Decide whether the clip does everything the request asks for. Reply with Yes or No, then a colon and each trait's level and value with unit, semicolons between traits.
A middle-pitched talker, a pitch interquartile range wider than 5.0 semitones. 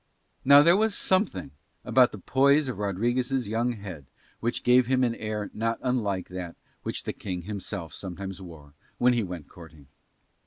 No: low, 110 Hz; wide, 5.6 semitones